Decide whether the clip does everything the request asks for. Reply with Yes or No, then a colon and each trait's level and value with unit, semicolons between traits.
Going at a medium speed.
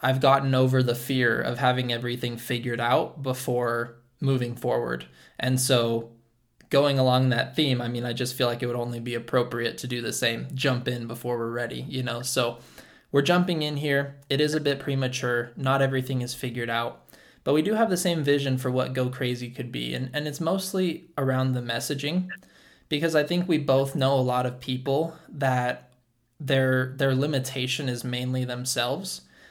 Yes: average, 190 wpm